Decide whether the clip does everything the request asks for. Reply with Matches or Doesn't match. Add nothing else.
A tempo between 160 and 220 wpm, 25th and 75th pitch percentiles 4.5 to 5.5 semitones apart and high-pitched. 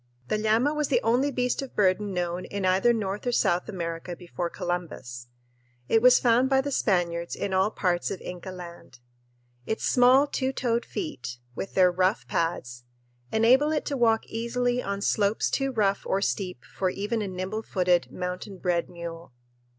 Matches